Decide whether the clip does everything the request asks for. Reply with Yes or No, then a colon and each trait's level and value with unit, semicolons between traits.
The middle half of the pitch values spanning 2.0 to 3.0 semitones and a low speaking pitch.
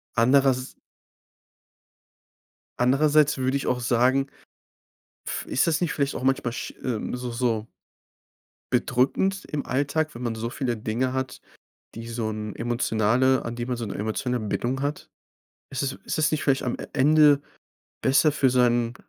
Yes: average, 2.7 semitones; low, 125 Hz